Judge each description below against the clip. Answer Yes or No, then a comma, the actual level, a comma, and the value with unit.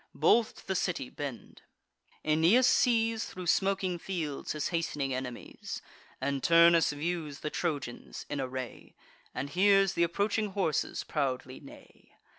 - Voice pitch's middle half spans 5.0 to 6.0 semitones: Yes, wide, 5.4 semitones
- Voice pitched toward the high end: No, medium, 165 Hz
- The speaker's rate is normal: No, slow, 130 wpm